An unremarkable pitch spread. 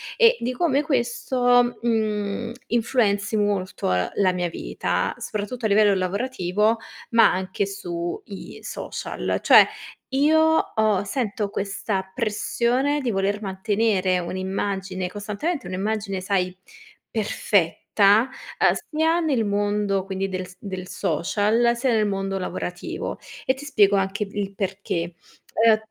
Yes: average, 3.6 semitones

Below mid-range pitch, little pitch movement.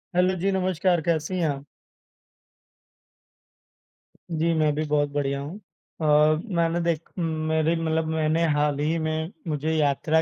No: medium, 160 Hz; narrow, 1.8 semitones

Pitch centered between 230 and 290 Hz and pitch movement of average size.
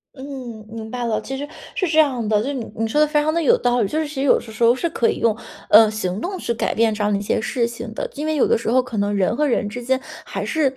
Yes: high, 240 Hz; average, 4.3 semitones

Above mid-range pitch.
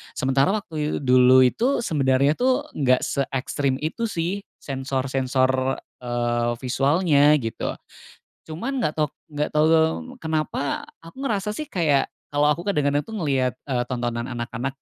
No: medium, 140 Hz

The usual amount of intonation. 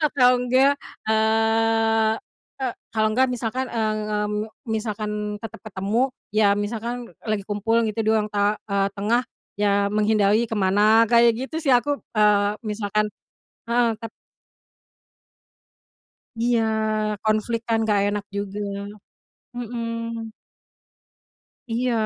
No: narrow, 2.0 semitones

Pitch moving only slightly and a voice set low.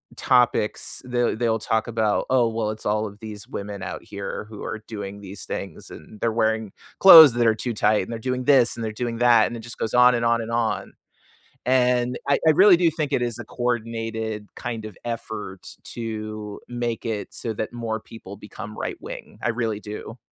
Yes: narrow, 2.2 semitones; low, 115 Hz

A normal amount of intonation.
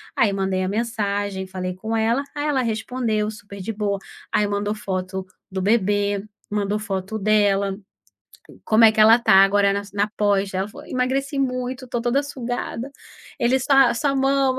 Yes: average, 3.7 semitones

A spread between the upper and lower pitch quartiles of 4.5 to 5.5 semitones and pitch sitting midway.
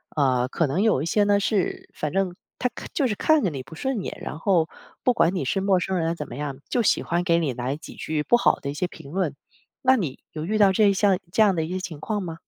Yes: average, 4.9 semitones; medium, 180 Hz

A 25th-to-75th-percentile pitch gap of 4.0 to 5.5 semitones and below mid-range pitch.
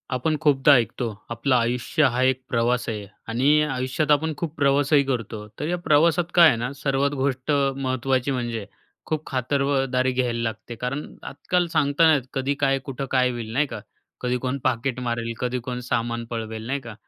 No: average, 2.9 semitones; low, 130 Hz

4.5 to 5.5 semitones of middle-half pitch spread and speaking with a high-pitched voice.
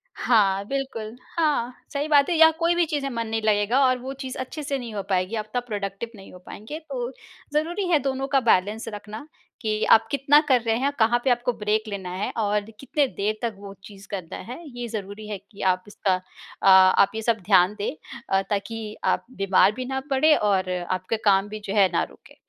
Yes: average, 4.8 semitones; high, 220 Hz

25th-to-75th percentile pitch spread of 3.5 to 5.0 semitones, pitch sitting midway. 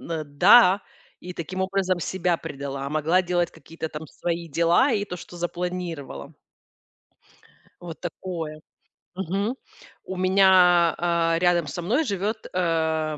No: narrow, 2.4 semitones; medium, 175 Hz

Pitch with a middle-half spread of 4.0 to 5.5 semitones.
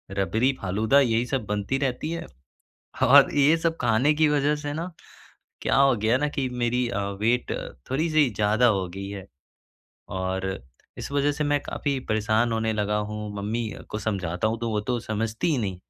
Yes: average, 5.1 semitones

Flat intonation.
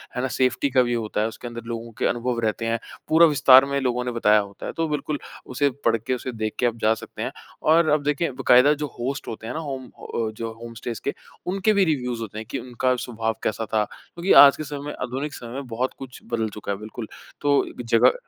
No: average, 3.7 semitones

